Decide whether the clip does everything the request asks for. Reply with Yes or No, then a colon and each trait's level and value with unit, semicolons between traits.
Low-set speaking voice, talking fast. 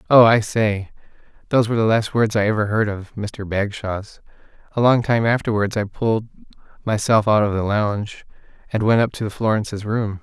No: low, 110 Hz; average, 180 wpm